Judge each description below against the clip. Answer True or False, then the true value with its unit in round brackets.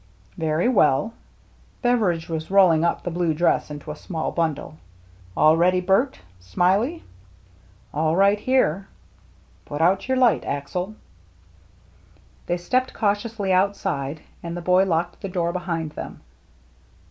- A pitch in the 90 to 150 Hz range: False (175 Hz)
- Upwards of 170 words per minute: False (135 wpm)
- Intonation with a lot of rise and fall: False (3.8 semitones)